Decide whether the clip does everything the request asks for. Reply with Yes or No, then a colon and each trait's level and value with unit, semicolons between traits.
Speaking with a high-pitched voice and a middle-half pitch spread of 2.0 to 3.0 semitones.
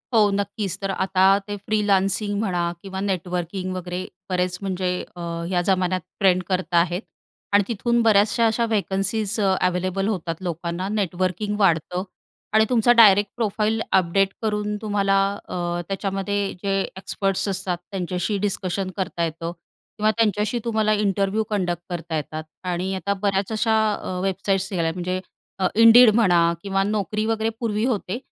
Yes: high, 195 Hz; narrow, 2.5 semitones